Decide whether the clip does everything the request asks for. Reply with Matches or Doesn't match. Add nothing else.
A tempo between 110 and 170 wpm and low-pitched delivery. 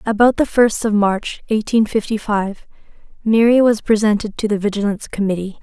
Doesn't match